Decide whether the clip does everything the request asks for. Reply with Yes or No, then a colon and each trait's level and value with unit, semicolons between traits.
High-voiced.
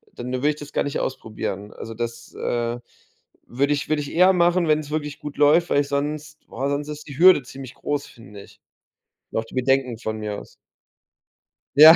No: medium, 140 Hz